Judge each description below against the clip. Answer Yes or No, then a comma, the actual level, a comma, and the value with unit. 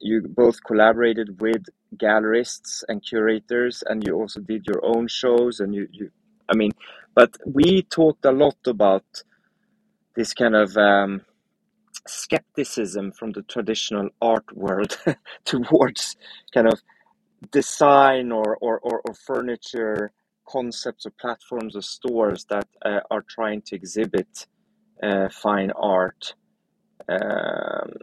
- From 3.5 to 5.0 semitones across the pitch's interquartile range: No, average, 2.9 semitones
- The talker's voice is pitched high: No, low, 115 Hz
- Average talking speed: No, slow, 125 wpm